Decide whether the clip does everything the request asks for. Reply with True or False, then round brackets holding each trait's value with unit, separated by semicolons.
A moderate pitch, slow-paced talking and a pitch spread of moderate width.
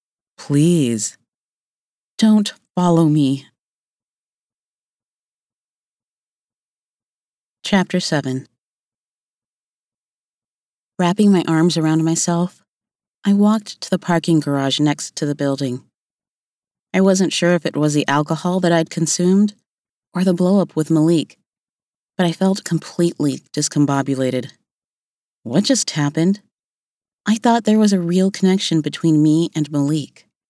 True (165 Hz; 110 wpm; 4.0 semitones)